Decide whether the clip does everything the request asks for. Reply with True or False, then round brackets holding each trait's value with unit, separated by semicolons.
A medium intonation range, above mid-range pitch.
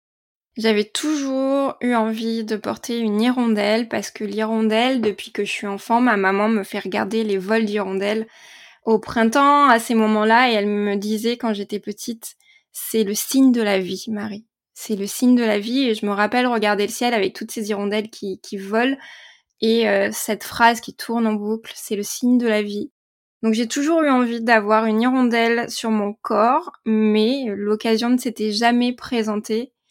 False (2.3 semitones; 225 Hz)